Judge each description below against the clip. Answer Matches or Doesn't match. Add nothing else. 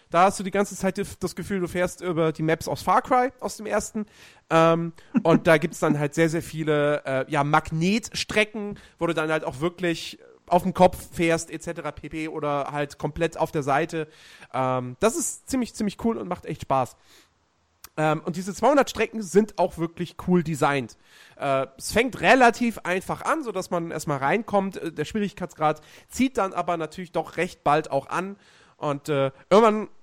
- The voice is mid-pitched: Matches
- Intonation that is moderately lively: Matches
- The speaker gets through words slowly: Doesn't match